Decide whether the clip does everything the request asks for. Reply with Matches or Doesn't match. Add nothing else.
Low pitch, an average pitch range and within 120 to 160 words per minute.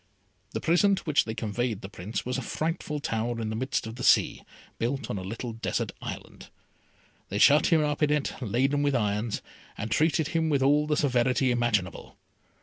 Doesn't match